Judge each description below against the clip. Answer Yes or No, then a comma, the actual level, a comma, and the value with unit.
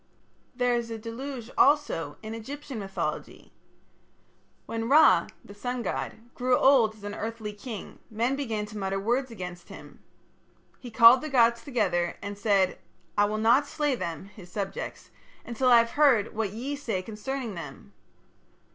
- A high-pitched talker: Yes, high, 230 Hz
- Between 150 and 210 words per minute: Yes, average, 155 wpm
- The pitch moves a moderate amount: Yes, average, 3.8 semitones